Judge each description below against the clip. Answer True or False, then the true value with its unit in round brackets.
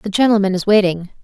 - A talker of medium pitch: False (200 Hz)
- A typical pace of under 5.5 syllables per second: False (6.4 syllables/s)